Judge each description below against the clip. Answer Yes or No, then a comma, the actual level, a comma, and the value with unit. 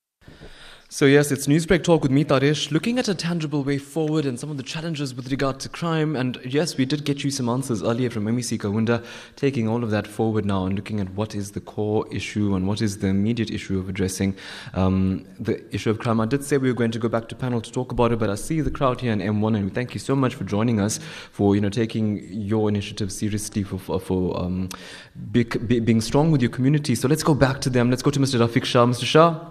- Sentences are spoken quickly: Yes, fast, 250 wpm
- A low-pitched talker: Yes, low, 120 Hz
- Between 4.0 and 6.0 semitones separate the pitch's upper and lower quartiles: Yes, average, 5.0 semitones